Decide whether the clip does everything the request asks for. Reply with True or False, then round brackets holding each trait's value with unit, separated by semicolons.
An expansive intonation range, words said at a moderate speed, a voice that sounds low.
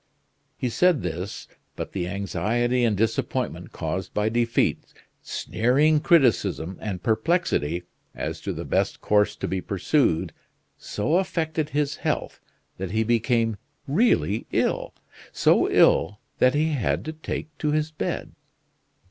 False (7.1 semitones; 130 wpm; 115 Hz)